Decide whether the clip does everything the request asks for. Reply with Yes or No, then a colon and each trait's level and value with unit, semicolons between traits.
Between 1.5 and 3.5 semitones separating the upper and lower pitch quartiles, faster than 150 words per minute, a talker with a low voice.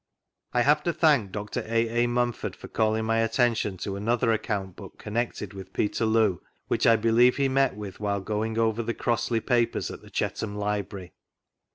Yes: narrow, 2.4 semitones; average, 180 wpm; low, 115 Hz